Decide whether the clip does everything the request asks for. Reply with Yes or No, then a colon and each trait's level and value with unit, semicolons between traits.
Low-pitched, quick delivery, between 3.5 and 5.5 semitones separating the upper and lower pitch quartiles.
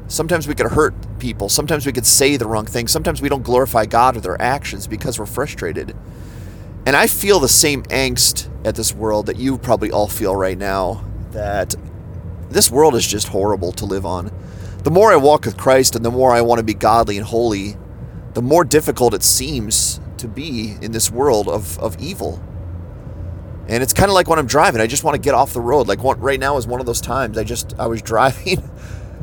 Yes: low, 115 Hz; fast, 220 wpm; average, 5.0 semitones